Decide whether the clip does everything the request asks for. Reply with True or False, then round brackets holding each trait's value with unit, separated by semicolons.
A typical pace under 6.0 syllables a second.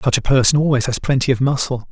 False (6.6 syllables/s)